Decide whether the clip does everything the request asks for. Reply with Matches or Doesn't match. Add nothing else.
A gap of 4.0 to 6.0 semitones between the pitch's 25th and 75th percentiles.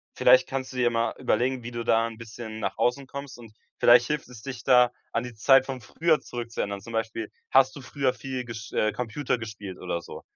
Doesn't match